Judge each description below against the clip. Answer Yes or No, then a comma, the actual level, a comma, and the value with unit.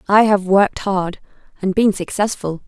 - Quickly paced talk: No, average, 155 wpm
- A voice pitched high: Yes, high, 195 Hz